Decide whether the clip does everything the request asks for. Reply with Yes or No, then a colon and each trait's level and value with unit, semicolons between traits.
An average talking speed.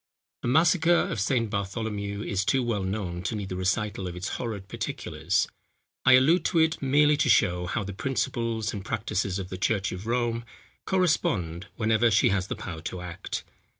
Yes: average, 185 wpm